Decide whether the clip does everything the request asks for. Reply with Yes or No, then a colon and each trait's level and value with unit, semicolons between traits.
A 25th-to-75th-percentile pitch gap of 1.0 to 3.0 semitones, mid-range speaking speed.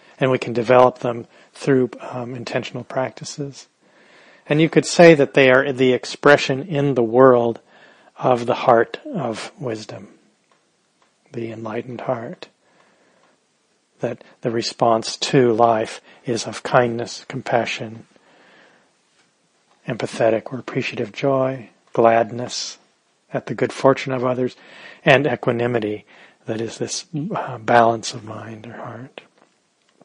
No: narrow, 2.4 semitones; slow, 120 wpm